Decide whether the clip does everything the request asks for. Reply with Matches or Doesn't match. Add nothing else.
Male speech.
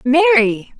Doesn't match